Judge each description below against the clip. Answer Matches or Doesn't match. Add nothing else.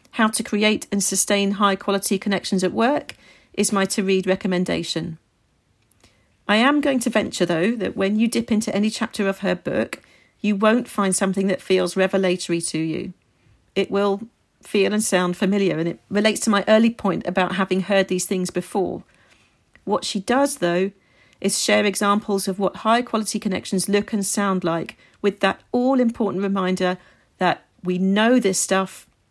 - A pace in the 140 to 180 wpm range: Matches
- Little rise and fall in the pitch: Matches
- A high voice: Matches